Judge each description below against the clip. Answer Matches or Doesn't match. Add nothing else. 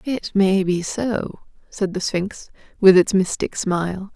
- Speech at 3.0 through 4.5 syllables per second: Matches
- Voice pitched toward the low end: Doesn't match